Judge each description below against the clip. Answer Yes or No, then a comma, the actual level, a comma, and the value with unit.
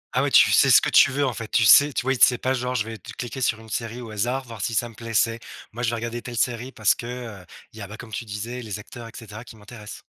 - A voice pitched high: No, low, 115 Hz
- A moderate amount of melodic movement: No, narrow, 2.1 semitones